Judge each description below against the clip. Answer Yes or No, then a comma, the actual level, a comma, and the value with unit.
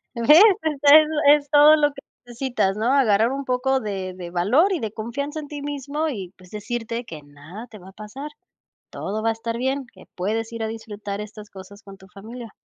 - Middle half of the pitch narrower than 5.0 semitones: No, average, 5.3 semitones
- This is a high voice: Yes, high, 230 Hz